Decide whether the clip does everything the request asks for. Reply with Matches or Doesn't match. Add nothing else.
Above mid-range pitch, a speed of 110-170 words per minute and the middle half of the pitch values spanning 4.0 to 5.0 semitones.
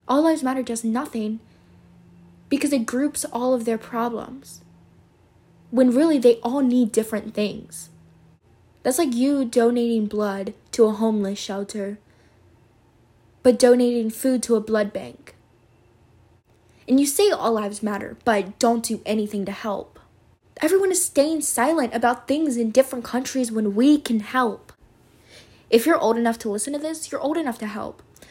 Matches